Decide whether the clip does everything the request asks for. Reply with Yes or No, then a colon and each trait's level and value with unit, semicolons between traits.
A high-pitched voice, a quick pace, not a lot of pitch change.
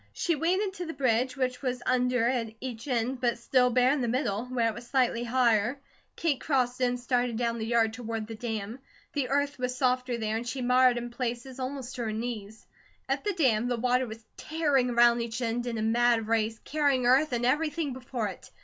Yes: high, 245 Hz; fast, 215 wpm; narrow, 2.0 semitones